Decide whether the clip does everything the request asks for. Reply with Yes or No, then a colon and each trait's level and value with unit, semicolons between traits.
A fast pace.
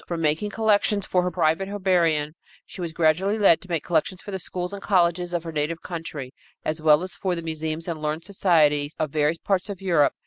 Yes: fast, 215 wpm